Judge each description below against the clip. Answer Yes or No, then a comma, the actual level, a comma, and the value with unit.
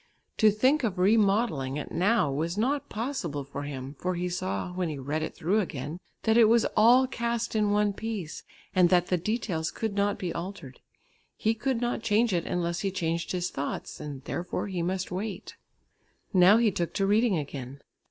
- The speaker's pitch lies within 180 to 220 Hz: Yes, medium, 185 Hz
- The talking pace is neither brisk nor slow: Yes, average, 190 wpm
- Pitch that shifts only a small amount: No, average, 5.1 semitones